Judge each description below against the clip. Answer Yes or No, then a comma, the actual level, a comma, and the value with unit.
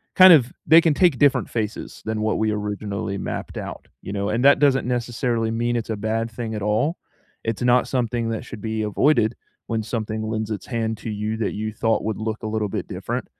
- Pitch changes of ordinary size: No, narrow, 2.0 semitones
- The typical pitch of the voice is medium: No, low, 110 Hz